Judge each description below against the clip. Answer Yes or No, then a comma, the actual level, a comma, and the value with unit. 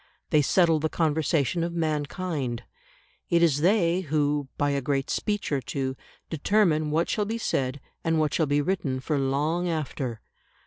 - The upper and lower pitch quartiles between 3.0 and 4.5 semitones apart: Yes, average, 3.3 semitones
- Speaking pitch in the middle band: Yes, medium, 155 Hz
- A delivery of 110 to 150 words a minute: No, average, 165 wpm